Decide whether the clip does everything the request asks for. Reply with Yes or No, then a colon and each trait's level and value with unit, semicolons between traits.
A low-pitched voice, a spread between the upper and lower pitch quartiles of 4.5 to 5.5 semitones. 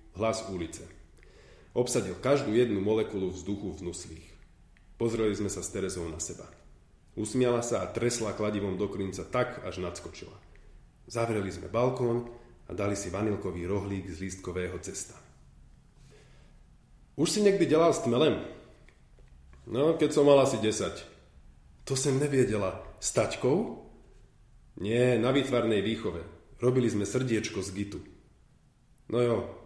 Yes: low, 100 Hz; average, 5.0 semitones